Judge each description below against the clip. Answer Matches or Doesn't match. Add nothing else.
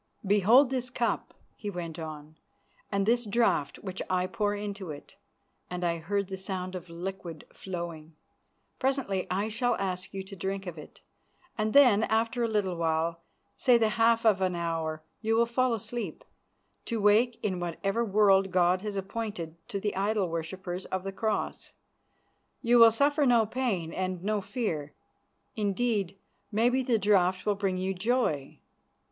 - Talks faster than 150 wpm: Matches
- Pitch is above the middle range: Matches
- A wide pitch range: Doesn't match